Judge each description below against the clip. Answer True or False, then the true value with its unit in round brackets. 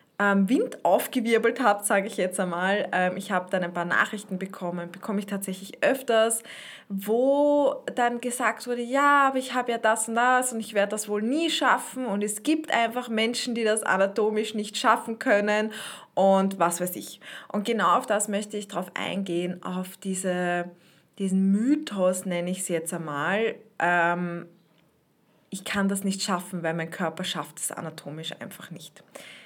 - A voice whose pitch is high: True (200 Hz)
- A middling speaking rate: True (165 wpm)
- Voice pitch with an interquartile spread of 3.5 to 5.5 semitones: True (4.0 semitones)